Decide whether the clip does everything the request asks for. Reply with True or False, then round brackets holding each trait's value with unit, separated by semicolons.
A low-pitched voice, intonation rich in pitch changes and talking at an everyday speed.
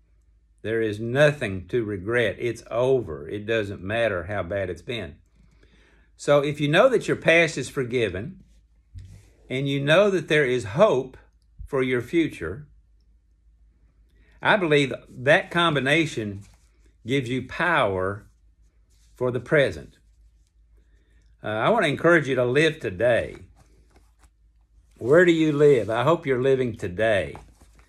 False (110 Hz; 8.6 semitones; 130 wpm)